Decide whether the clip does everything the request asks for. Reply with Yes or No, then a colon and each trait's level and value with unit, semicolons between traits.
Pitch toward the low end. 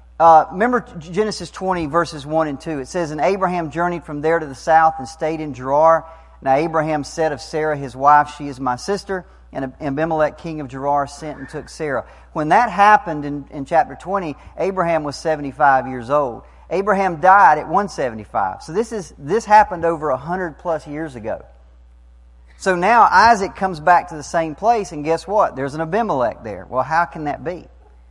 No: medium, 160 Hz